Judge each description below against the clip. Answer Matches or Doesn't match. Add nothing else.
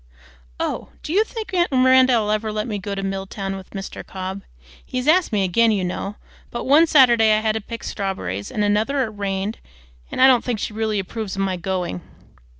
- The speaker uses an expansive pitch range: Doesn't match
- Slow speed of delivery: Doesn't match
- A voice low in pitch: Doesn't match